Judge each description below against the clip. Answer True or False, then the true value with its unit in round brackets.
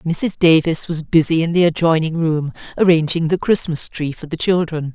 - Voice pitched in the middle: True (165 Hz)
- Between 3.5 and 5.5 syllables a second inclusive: True (5.0 syllables/s)